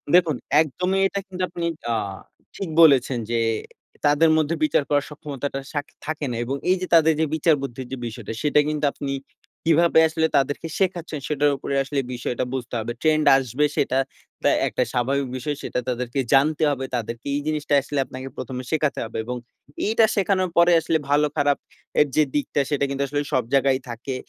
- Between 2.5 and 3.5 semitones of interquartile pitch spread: Yes, average, 3.1 semitones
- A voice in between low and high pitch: Yes, medium, 145 Hz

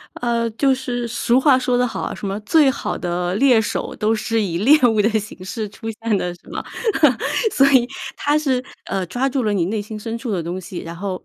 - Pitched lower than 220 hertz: No, high, 225 Hz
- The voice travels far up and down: No, average, 4.2 semitones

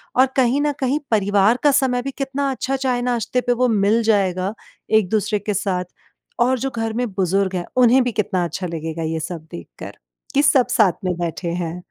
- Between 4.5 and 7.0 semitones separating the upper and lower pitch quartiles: Yes, wide, 5.4 semitones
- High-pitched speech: Yes, high, 220 Hz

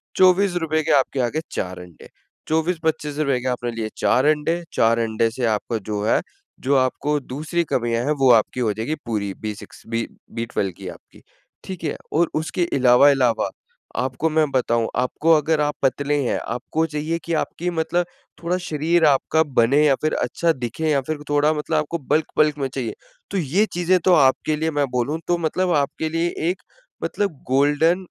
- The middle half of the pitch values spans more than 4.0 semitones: Yes, average, 4.4 semitones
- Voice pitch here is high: No, medium, 150 Hz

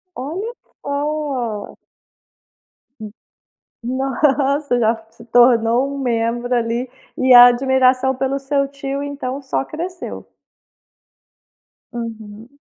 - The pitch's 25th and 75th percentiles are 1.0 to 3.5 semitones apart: Yes, average, 2.7 semitones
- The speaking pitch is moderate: No, very high, 260 Hz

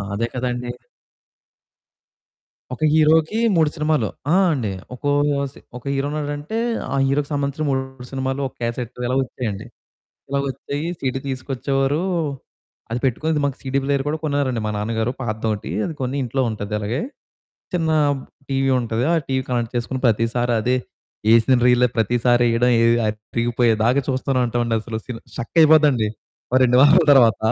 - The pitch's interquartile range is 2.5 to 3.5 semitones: Yes, average, 3.2 semitones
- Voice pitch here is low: Yes, low, 130 Hz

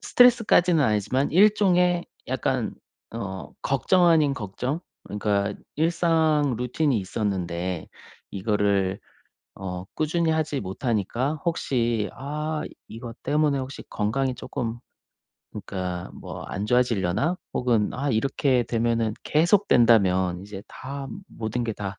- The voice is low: Yes, low, 120 Hz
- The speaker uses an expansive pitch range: Yes, wide, 6.8 semitones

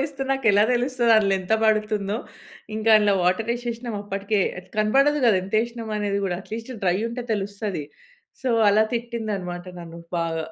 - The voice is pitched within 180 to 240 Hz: Yes, high, 215 Hz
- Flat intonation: No, average, 3.0 semitones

